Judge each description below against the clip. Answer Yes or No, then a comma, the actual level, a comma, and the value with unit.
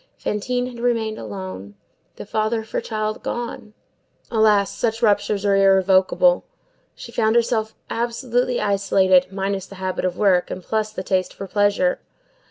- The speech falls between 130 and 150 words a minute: Yes, average, 140 wpm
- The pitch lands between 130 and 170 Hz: No, high, 210 Hz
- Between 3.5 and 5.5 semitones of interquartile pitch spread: No, average, 3.1 semitones